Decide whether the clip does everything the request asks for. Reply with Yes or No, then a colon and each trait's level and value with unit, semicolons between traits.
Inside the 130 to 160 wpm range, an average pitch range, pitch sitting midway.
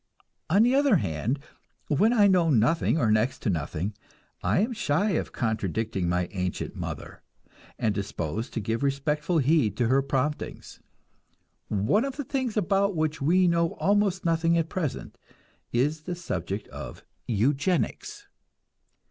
No: average, 145 wpm; wide, 8.7 semitones; medium, 150 Hz